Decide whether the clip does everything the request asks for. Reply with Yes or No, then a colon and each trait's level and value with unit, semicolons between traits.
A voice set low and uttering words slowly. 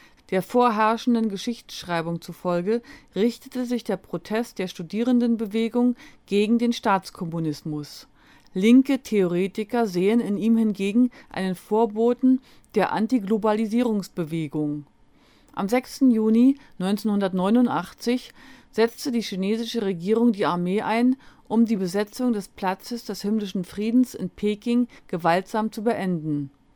No: high, 220 Hz; slow, 105 wpm